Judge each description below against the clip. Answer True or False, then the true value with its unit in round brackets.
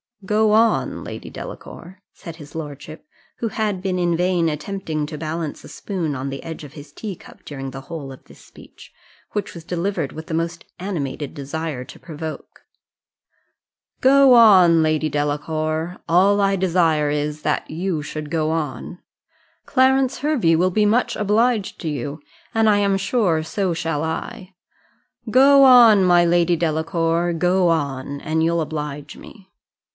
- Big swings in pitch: False (4.3 semitones)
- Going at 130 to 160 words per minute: True (155 wpm)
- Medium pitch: True (165 Hz)